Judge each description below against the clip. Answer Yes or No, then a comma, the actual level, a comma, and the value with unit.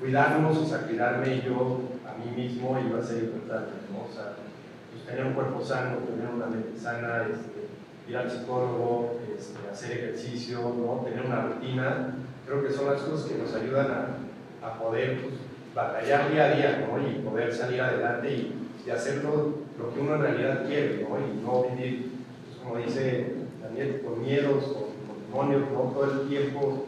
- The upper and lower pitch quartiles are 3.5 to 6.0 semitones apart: No, narrow, 2.5 semitones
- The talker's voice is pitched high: No, low, 125 Hz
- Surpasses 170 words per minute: Yes, average, 185 wpm